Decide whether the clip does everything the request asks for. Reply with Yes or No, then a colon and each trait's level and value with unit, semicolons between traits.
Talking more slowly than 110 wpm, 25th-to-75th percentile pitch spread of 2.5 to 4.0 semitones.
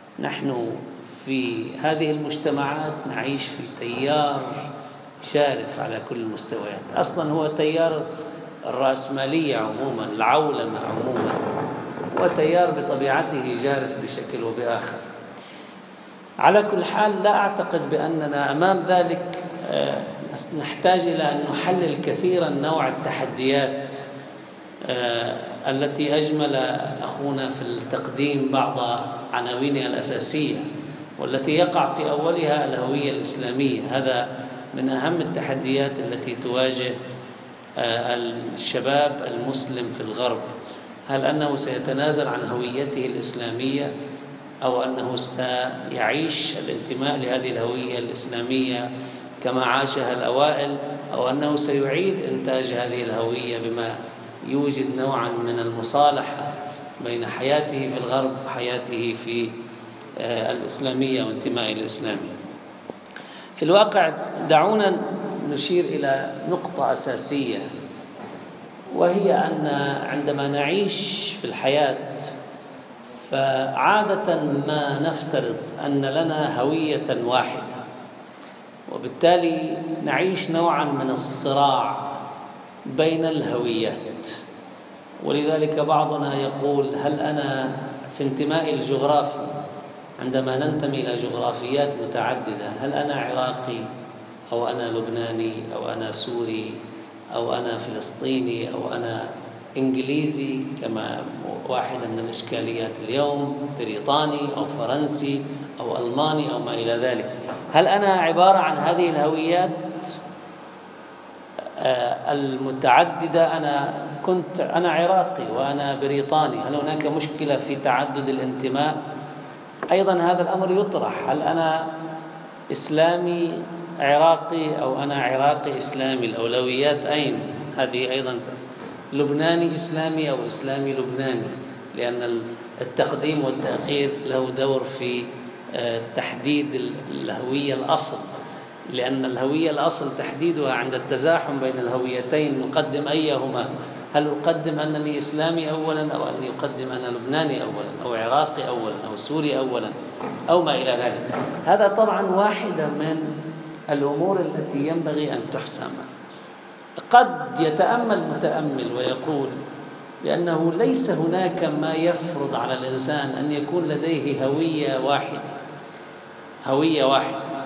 Yes: average, 100 wpm; average, 3.2 semitones